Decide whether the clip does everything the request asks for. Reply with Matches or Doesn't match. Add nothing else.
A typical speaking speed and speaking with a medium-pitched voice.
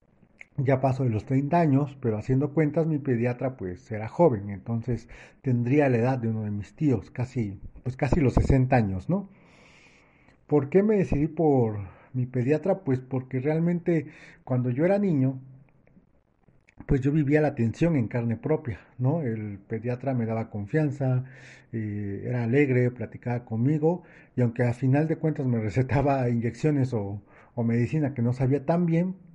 Doesn't match